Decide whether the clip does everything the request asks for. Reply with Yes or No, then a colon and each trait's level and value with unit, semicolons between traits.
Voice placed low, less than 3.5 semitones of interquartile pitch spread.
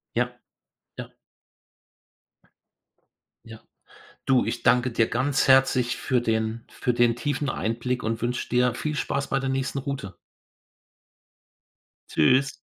Yes: low, 125 Hz; narrow, 2.4 semitones